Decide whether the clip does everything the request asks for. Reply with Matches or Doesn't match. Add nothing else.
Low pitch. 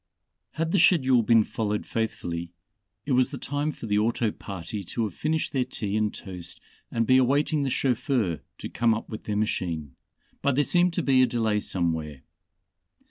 Matches